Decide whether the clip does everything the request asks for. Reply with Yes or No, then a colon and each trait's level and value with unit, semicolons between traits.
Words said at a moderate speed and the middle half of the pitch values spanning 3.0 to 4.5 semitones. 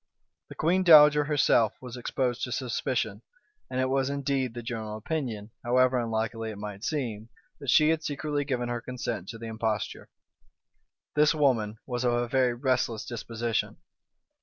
Yes: average, 160 wpm; average, 3.5 semitones